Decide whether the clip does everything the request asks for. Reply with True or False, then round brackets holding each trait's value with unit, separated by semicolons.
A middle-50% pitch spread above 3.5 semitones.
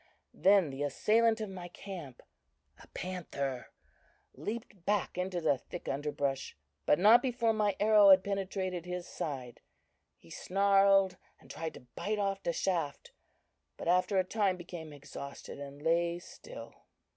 True (4.6 semitones)